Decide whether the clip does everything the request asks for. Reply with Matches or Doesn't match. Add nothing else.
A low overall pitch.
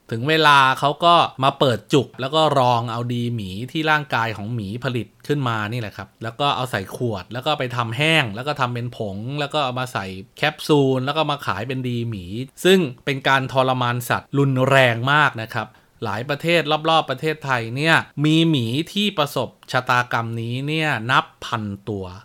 Matches